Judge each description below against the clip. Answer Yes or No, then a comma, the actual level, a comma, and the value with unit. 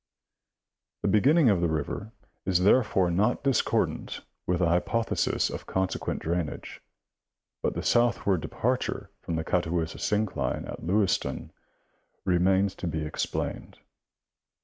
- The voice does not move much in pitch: No, average, 3.7 semitones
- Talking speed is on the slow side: Yes, slow, 120 wpm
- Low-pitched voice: Yes, very low, 95 Hz